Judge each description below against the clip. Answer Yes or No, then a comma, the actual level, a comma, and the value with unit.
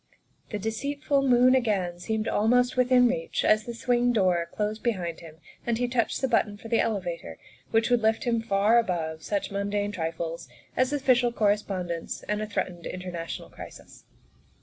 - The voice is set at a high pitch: Yes, high, 215 Hz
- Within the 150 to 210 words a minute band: Yes, average, 170 wpm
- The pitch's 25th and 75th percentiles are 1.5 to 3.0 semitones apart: No, average, 4.9 semitones